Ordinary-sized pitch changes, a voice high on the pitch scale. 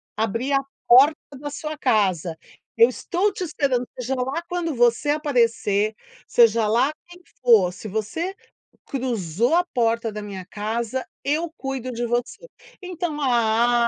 Yes: average, 4.9 semitones; high, 245 Hz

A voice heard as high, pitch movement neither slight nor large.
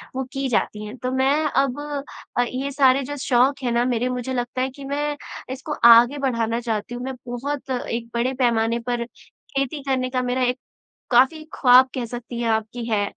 No: very high, 255 Hz; narrow, 2.1 semitones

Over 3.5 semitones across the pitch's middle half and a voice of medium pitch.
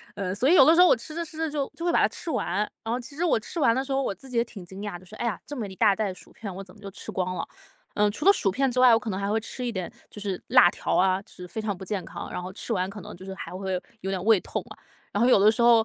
No: average, 4.8 semitones; high, 210 Hz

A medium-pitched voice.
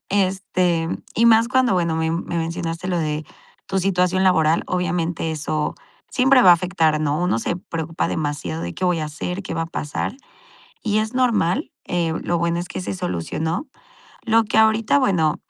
Yes: medium, 175 Hz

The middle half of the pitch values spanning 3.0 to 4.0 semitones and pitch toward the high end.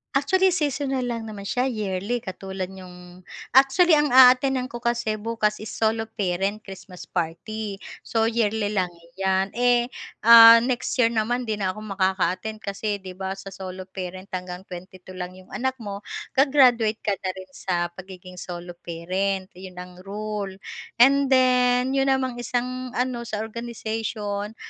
No: average, 4.5 semitones; high, 215 Hz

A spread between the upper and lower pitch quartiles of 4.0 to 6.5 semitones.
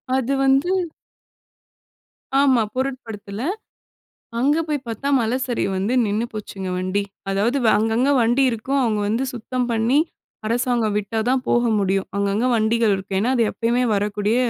No: average, 3.5 semitones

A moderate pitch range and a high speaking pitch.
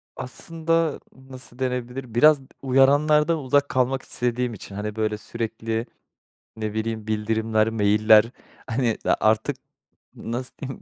No: average, 3.4 semitones; low, 120 Hz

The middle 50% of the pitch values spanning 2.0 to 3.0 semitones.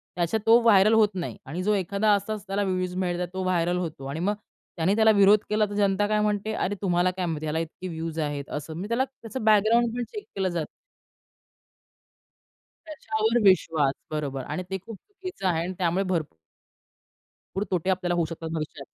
No: average, 4.1 semitones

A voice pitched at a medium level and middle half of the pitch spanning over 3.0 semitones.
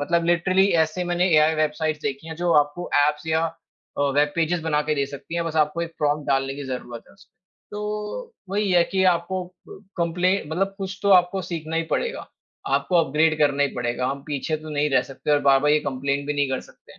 Yes: medium, 160 Hz; average, 3.4 semitones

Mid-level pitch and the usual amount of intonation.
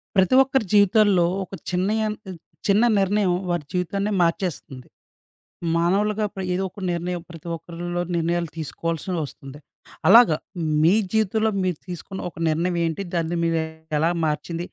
Yes: medium, 180 Hz; average, 3.2 semitones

